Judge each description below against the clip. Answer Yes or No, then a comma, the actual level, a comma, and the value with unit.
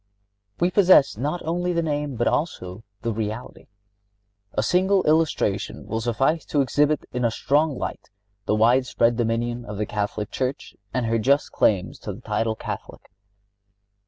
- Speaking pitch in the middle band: No, low, 125 Hz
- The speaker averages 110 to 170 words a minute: Yes, average, 160 wpm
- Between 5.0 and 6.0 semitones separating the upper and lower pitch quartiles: Yes, average, 5.3 semitones